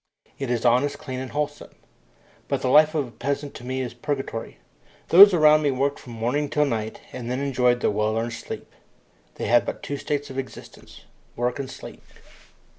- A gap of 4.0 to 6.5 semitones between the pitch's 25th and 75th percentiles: No, average, 3.0 semitones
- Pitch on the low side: Yes, low, 130 Hz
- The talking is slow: No, average, 190 wpm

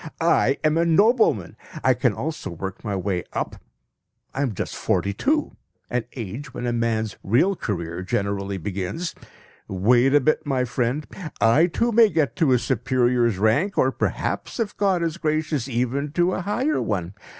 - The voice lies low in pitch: Yes, low, 125 Hz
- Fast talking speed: No, average, 170 wpm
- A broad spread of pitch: Yes, wide, 7.6 semitones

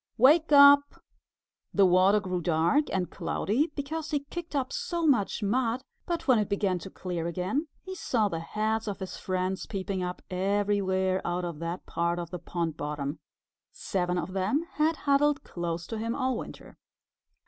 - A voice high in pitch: Yes, high, 200 Hz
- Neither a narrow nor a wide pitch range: No, wide, 7.4 semitones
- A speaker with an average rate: Yes, average, 170 wpm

